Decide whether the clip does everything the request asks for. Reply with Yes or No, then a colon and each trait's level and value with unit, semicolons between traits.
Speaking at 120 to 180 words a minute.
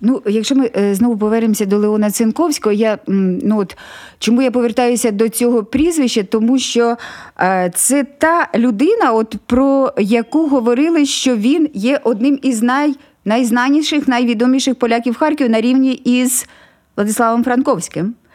Yes: average, 135 wpm